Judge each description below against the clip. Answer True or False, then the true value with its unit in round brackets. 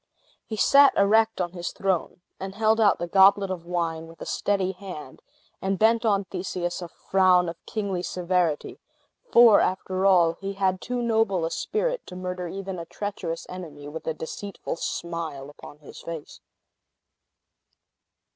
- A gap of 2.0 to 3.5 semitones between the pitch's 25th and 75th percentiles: True (2.9 semitones)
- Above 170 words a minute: False (155 wpm)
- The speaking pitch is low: False (185 Hz)